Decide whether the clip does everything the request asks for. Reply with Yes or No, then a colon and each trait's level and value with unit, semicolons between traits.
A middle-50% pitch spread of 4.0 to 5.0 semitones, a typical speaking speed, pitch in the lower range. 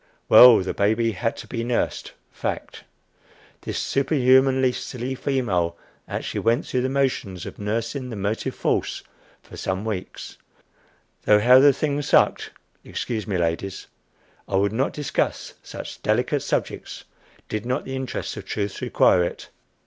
Yes: average, 4.5 semitones; average, 145 wpm; low, 115 Hz